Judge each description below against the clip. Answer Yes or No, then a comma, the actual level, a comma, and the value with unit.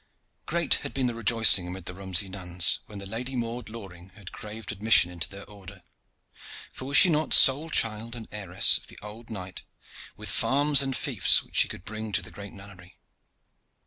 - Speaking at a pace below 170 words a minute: No, average, 190 wpm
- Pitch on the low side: Yes, low, 105 Hz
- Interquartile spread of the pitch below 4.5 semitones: Yes, average, 4.0 semitones